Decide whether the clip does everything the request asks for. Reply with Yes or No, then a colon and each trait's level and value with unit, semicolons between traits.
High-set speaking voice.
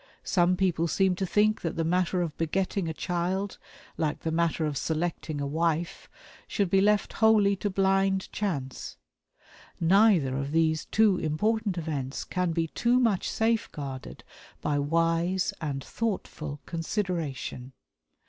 No: medium, 175 Hz